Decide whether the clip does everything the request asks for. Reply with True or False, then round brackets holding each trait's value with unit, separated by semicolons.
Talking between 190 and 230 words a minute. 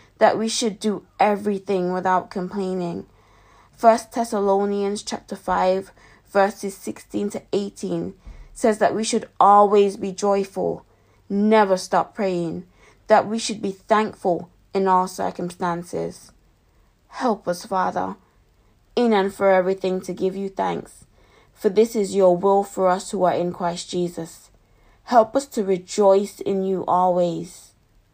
False (135 wpm)